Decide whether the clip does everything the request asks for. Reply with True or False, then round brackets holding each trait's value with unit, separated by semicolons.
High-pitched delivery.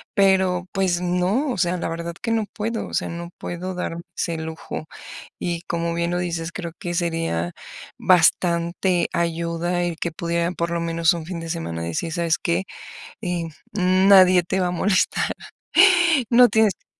False (175 Hz)